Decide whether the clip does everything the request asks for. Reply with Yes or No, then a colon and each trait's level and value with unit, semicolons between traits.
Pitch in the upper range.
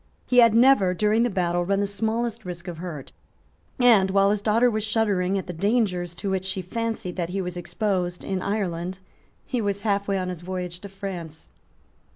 Yes: high, 195 Hz